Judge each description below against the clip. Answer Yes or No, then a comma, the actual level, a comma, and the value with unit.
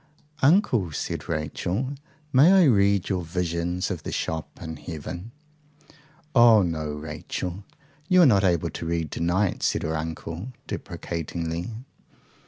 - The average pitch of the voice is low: Yes, very low, 85 Hz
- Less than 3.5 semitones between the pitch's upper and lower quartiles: No, average, 4.5 semitones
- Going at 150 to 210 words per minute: No, slow, 135 wpm